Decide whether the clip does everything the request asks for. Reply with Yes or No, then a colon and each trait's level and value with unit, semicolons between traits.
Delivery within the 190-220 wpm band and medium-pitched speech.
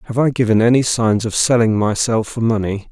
No: fast, 205 wpm; low, 115 Hz